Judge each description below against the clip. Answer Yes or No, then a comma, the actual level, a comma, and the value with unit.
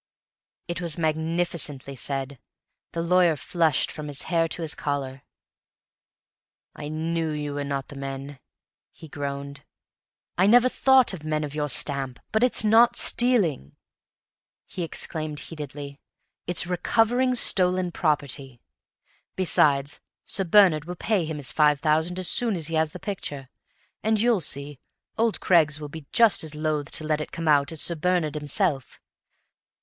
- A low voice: No, medium, 155 Hz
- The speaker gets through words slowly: No, average, 155 wpm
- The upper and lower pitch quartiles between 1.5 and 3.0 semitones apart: No, average, 3.9 semitones